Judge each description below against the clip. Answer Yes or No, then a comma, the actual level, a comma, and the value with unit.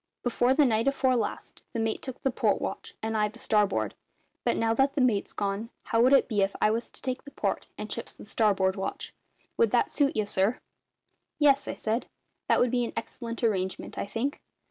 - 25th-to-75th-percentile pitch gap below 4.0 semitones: Yes, average, 3.4 semitones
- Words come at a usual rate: No, fast, 215 wpm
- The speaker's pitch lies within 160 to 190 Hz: No, high, 230 Hz